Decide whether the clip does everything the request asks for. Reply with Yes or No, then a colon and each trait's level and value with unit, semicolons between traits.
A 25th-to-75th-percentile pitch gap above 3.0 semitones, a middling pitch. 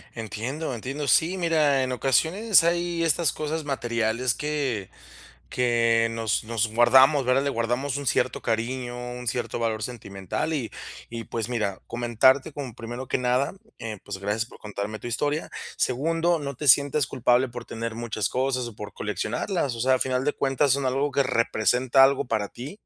No: average, 3.5 semitones; low, 125 Hz